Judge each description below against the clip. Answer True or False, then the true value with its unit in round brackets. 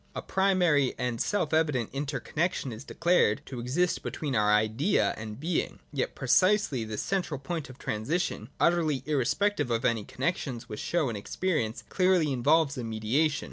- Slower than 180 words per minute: True (165 wpm)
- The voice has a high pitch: False (140 Hz)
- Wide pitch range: True (6.4 semitones)